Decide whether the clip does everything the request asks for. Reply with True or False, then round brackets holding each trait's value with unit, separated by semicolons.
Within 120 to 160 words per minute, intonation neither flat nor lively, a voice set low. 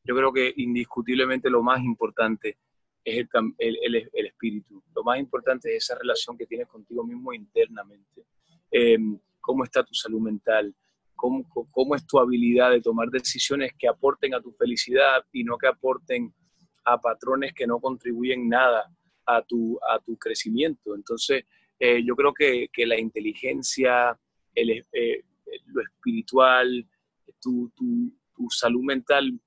False (155 wpm; 7.3 semitones; 130 Hz)